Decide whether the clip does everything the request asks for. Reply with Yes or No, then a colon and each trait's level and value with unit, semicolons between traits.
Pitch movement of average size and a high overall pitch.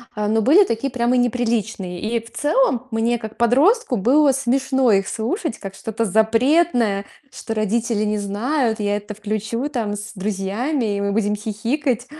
Yes: average, 3.5 semitones; high, 225 Hz